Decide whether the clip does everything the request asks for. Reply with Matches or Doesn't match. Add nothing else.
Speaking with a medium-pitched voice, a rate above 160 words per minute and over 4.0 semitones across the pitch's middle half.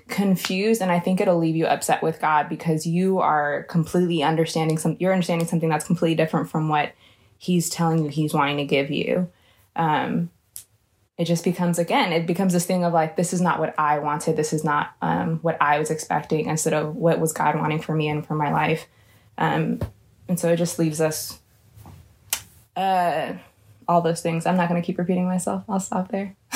Doesn't match